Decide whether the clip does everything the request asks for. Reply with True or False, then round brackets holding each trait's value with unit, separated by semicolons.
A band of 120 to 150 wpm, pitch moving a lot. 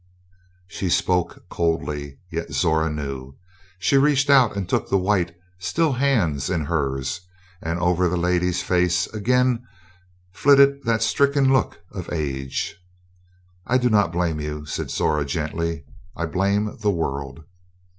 True (135 wpm; 6.0 semitones)